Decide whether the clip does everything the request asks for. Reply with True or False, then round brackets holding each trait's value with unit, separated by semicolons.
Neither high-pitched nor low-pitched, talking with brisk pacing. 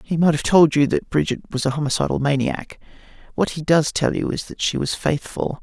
True (145 Hz; 225 wpm)